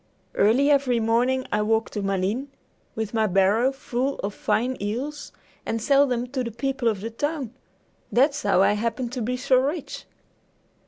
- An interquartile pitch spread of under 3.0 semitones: No, average, 3.6 semitones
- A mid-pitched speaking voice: No, high, 240 Hz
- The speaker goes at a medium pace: Yes, average, 170 wpm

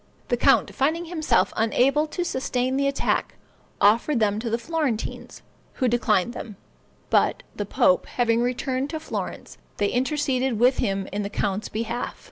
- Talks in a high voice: Yes, high, 245 Hz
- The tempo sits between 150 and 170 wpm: Yes, average, 155 wpm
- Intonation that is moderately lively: Yes, average, 4.2 semitones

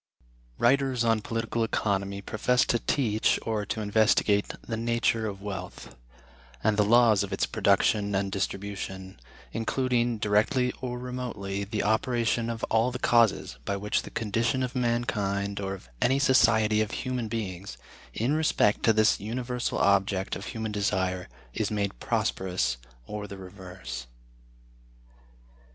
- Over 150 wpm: No, average, 140 wpm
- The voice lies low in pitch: Yes, low, 110 Hz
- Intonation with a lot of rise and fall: No, average, 3.0 semitones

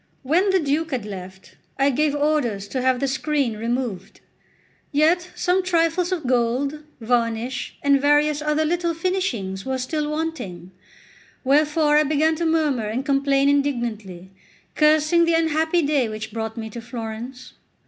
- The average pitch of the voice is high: Yes, very high, 280 Hz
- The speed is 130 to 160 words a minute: Yes, average, 150 wpm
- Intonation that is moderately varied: Yes, average, 4.9 semitones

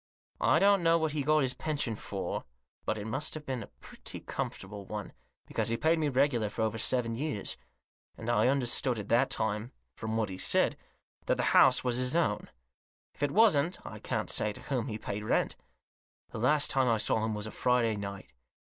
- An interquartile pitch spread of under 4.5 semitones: No, average, 4.9 semitones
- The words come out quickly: Yes, fast, 210 wpm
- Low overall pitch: Yes, low, 120 Hz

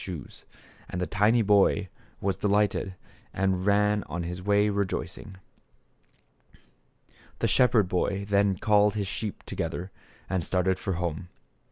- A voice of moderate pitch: No, low, 100 Hz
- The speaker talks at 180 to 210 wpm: No, average, 140 wpm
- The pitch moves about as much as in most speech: No, narrow, 2.1 semitones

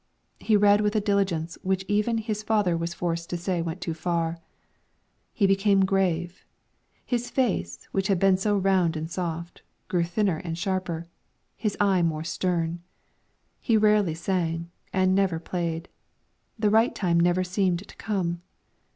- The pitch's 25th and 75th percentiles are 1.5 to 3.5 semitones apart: Yes, average, 3.2 semitones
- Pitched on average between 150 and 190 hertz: Yes, medium, 185 Hz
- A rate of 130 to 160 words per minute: Yes, average, 155 wpm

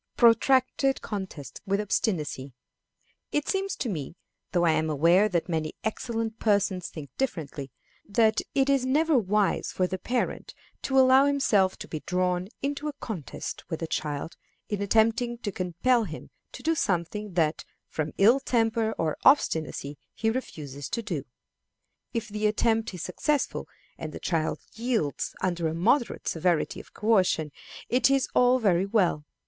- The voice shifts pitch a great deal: Yes, wide, 6.3 semitones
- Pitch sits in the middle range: No, high, 205 Hz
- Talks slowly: No, average, 155 wpm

